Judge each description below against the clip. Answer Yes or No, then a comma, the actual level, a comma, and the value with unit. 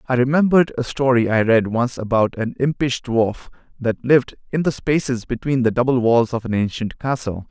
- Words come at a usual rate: Yes, average, 190 wpm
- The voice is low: Yes, low, 125 Hz